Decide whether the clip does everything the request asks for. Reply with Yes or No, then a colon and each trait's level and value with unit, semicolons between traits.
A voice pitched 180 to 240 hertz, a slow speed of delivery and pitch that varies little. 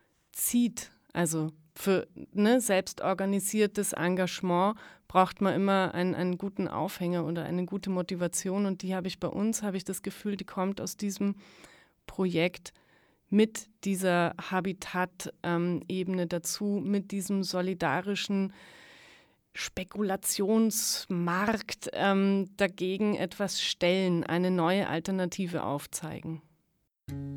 Yes: medium, 185 Hz; slow, 105 wpm; narrow, 2.3 semitones